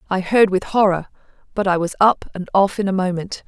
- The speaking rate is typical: No, fast, 225 wpm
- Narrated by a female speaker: Yes, female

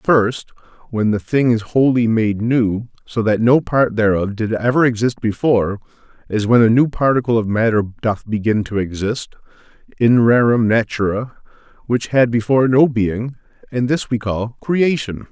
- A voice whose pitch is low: Yes, low, 115 Hz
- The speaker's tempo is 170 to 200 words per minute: No, average, 160 wpm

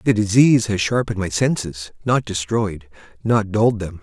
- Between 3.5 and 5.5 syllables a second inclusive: Yes, 5.1 syllables/s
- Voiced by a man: Yes, male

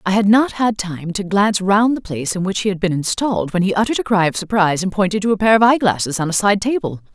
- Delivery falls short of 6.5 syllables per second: No, 6.6 syllables/s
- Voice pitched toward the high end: Yes, high, 195 Hz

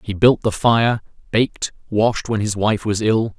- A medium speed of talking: Yes, average, 195 wpm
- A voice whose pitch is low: Yes, low, 110 Hz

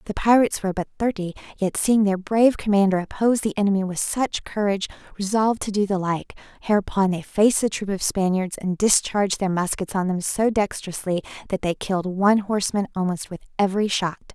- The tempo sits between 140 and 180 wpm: No, average, 190 wpm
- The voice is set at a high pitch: Yes, high, 200 Hz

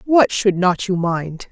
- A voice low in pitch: No, high, 190 Hz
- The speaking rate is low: No, average, 200 wpm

